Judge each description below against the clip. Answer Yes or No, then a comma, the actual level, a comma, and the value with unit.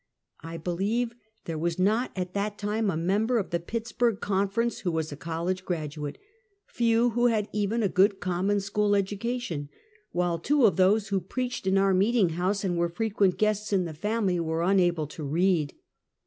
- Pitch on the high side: Yes, high, 195 Hz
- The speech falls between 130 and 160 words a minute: No, average, 185 wpm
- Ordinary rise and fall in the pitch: Yes, average, 3.8 semitones